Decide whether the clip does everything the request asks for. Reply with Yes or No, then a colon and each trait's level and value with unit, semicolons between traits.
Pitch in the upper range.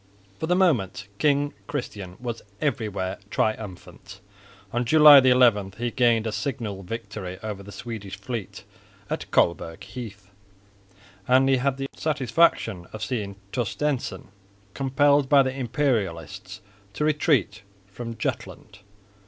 No: low, 120 Hz